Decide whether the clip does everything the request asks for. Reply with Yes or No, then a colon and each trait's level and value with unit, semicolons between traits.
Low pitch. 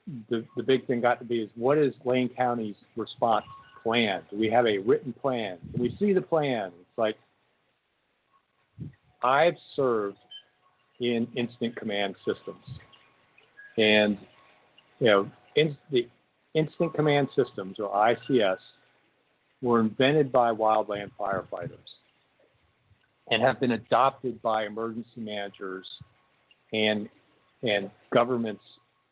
Yes: low, 120 Hz